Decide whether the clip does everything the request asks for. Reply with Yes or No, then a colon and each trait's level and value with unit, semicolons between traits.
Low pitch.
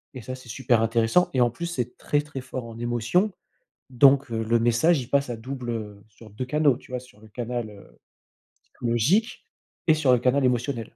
Yes: low, 125 Hz